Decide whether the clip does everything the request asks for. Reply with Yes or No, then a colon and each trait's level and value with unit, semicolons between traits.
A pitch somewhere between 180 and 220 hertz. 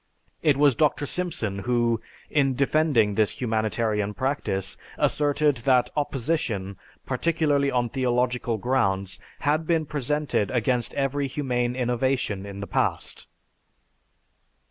No: low, 125 Hz